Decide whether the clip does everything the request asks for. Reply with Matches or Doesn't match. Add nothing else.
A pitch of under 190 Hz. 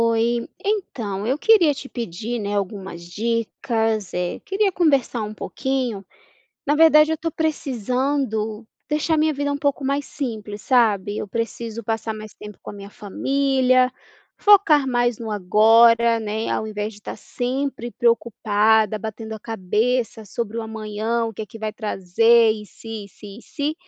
Doesn't match